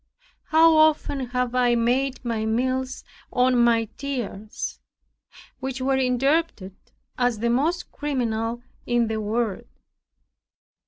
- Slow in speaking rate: Yes, slow, 110 wpm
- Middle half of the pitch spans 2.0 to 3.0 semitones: Yes, narrow, 2.5 semitones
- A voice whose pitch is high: Yes, very high, 250 Hz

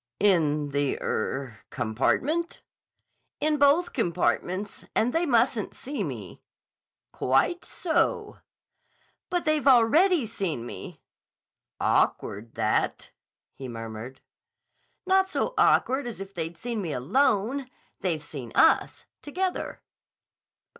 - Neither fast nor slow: No, slow, 100 wpm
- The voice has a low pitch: No, high, 210 Hz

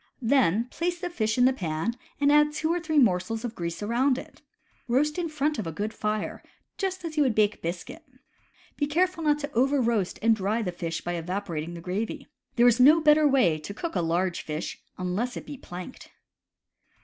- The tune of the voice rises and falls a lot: Yes, wide, 8.4 semitones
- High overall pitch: Yes, high, 235 Hz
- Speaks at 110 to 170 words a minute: No, average, 200 wpm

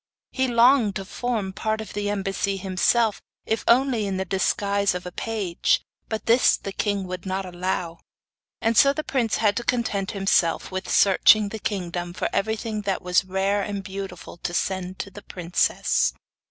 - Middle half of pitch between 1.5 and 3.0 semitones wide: Yes, average, 2.7 semitones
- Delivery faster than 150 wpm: Yes, average, 175 wpm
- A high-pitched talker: Yes, high, 200 Hz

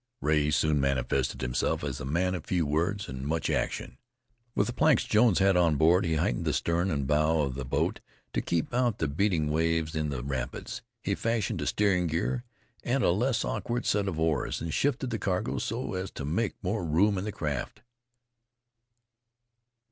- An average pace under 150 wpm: No, average, 190 wpm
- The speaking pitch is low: Yes, very low, 85 Hz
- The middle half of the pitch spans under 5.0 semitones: No, average, 5.3 semitones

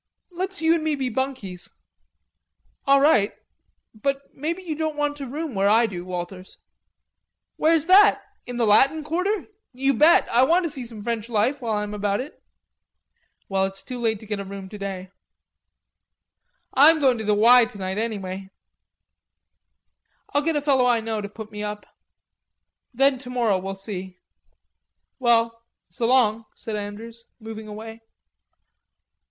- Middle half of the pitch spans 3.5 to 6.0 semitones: Yes, average, 5.0 semitones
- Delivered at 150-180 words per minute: Yes, average, 160 wpm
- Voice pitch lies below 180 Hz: No, high, 230 Hz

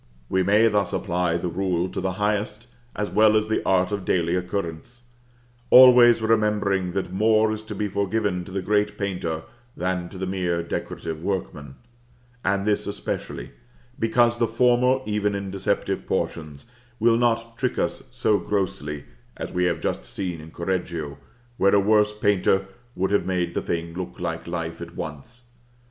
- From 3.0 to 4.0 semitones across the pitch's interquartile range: Yes, average, 3.4 semitones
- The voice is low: Yes, very low, 95 Hz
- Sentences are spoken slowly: No, average, 165 wpm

